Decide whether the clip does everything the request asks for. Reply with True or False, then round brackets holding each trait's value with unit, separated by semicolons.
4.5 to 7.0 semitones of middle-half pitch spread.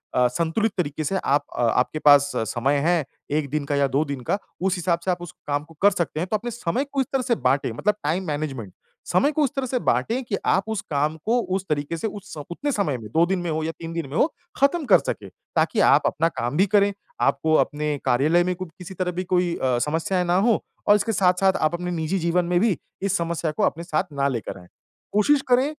True (5.0 semitones)